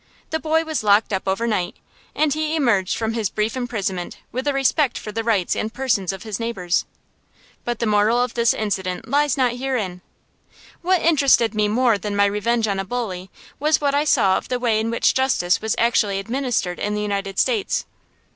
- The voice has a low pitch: No, high, 225 Hz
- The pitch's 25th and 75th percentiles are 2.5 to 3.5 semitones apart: No, average, 4.5 semitones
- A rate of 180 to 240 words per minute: Yes, average, 195 wpm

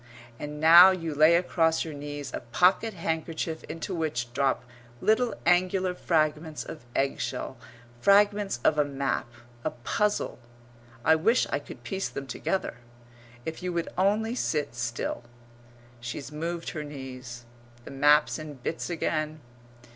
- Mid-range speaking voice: Yes, medium, 160 Hz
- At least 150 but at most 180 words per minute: No, average, 140 wpm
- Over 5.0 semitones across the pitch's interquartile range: No, average, 4.2 semitones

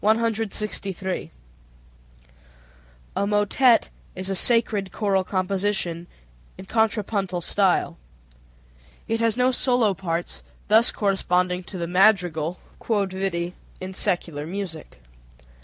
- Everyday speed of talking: No, slow, 90 wpm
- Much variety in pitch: No, average, 3.0 semitones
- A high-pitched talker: Yes, high, 195 Hz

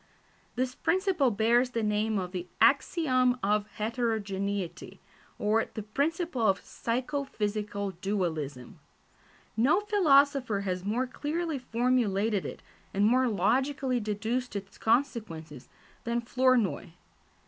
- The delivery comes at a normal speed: No, slow, 110 wpm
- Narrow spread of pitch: No, average, 4.2 semitones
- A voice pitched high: Yes, high, 225 Hz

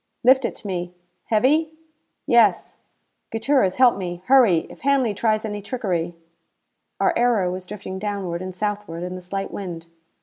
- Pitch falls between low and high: No, high, 205 Hz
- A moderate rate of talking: Yes, average, 160 wpm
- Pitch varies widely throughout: No, average, 4.7 semitones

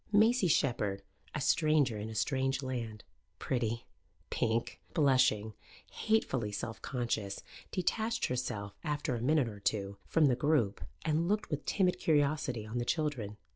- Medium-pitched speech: No, low, 130 Hz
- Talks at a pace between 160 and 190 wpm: No, average, 140 wpm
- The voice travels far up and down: Yes, wide, 5.8 semitones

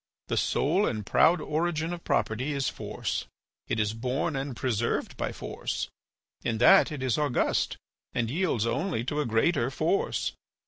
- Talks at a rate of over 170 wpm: No, average, 155 wpm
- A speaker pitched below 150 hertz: Yes, low, 135 Hz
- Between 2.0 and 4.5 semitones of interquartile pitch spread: No, wide, 5.4 semitones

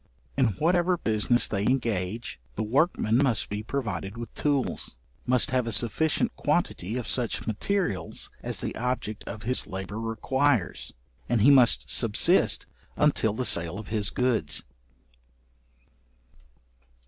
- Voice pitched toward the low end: Yes, low, 115 Hz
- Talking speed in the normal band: No, slow, 130 wpm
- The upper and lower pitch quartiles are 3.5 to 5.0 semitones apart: Yes, average, 3.8 semitones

